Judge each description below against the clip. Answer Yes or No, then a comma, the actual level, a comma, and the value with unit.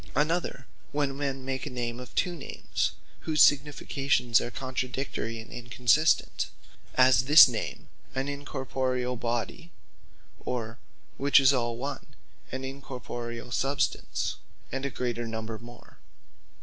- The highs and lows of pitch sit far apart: No, narrow, 2.6 semitones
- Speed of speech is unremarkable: No, slow, 125 wpm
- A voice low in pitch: Yes, low, 130 Hz